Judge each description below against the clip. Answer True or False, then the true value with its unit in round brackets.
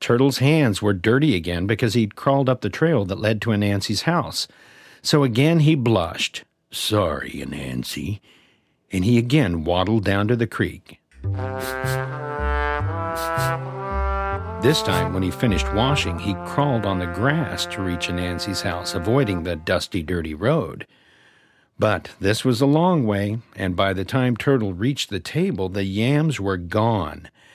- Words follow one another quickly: False (150 wpm)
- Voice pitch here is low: True (100 Hz)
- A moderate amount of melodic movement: False (6.9 semitones)